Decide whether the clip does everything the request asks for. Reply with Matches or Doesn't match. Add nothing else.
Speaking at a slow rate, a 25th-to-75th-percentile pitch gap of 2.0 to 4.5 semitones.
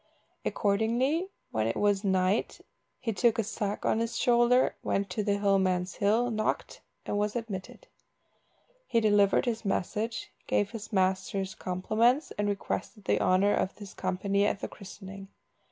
Doesn't match